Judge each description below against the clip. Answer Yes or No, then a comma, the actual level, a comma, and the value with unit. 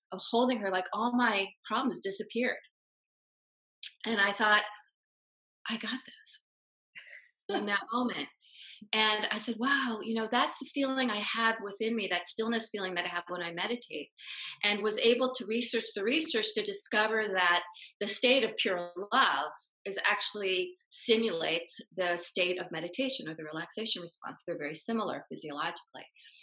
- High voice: Yes, high, 220 Hz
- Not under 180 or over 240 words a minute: No, average, 155 wpm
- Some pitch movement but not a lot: Yes, average, 4.1 semitones